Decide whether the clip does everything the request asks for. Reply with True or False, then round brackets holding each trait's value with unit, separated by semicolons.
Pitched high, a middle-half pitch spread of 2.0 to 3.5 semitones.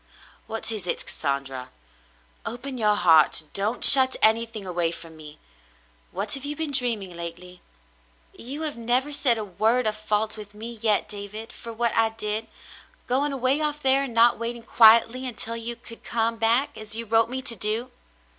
True (225 Hz; 2.9 semitones)